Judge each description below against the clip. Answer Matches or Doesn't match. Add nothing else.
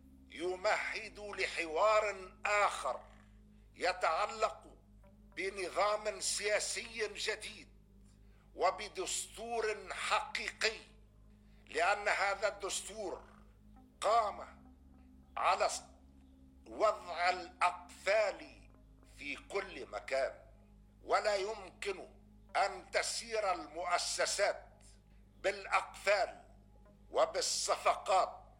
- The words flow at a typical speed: Doesn't match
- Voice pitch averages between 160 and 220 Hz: Matches